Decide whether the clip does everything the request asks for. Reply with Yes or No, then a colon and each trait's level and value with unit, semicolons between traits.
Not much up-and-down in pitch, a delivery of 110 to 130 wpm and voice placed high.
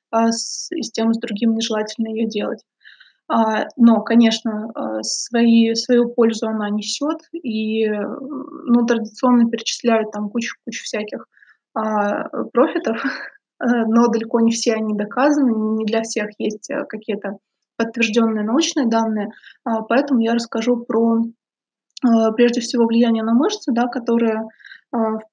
Yes: narrow, 1.7 semitones; average, 120 wpm; high, 230 Hz